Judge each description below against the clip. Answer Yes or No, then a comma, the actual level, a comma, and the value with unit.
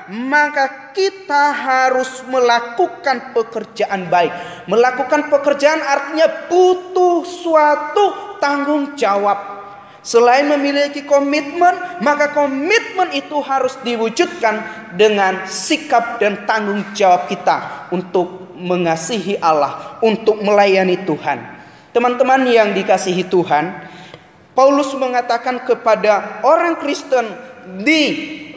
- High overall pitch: Yes, high, 245 Hz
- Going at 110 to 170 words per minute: No, average, 90 wpm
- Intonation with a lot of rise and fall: Yes, wide, 6.6 semitones